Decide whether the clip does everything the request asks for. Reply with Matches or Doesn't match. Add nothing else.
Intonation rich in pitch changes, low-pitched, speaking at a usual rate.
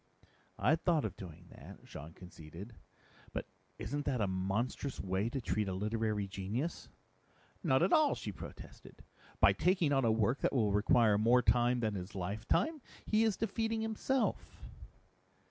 Matches